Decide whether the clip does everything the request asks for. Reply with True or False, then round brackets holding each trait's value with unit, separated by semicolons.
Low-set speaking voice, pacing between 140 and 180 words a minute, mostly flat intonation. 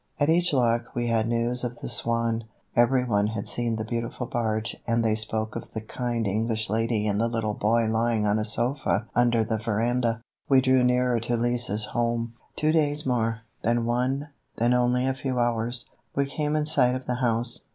False (120 Hz; 195 wpm; 1.8 semitones)